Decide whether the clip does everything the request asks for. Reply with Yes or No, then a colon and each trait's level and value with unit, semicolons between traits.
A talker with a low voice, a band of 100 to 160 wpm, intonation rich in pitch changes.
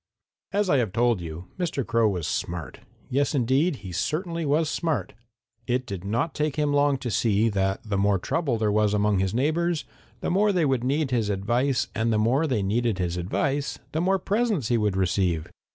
No: low, 120 Hz; average, 200 wpm; wide, 6.7 semitones